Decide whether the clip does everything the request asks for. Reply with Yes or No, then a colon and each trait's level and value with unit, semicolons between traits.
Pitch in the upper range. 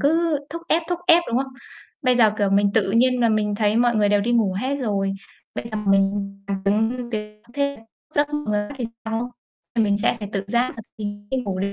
Yes: high, 220 Hz